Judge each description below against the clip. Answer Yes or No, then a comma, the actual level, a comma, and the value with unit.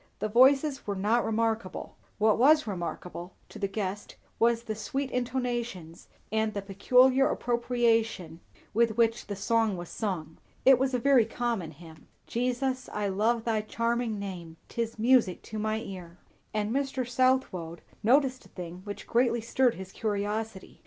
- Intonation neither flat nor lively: Yes, average, 3.6 semitones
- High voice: Yes, high, 225 Hz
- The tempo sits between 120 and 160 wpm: Yes, average, 150 wpm